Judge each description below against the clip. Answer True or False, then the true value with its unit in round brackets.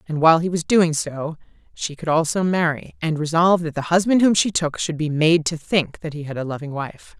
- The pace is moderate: False (240 wpm)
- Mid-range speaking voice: True (160 Hz)